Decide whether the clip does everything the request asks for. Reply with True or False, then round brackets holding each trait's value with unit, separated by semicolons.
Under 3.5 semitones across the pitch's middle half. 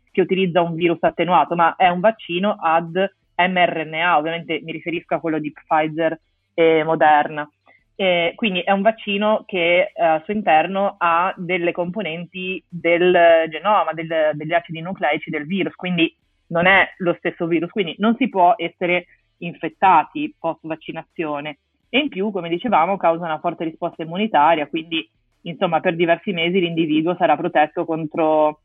True (2.5 semitones)